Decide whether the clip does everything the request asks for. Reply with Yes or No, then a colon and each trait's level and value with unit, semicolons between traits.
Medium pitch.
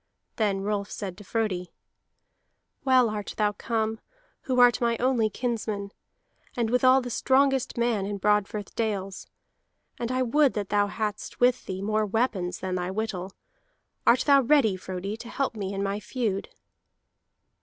No: high, 215 Hz